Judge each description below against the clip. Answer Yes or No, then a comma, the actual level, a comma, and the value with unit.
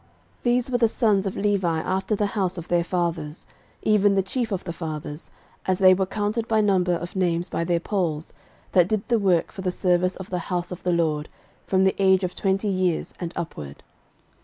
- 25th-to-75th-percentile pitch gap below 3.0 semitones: Yes, narrow, 2.5 semitones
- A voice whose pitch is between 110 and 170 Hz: No, medium, 185 Hz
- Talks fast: Yes, fast, 210 wpm